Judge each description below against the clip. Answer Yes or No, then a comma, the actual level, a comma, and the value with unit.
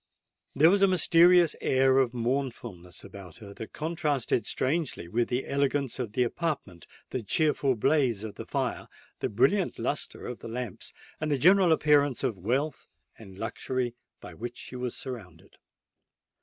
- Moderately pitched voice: No, low, 130 Hz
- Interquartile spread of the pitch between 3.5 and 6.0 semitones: Yes, average, 4.8 semitones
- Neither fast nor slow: Yes, average, 155 wpm